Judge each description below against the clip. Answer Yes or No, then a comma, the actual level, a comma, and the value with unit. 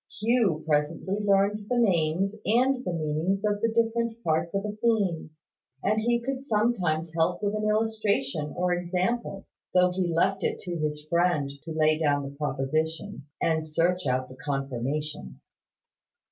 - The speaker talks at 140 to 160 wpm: Yes, average, 155 wpm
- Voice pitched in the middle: Yes, medium, 180 Hz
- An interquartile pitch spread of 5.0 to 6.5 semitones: Yes, wide, 5.4 semitones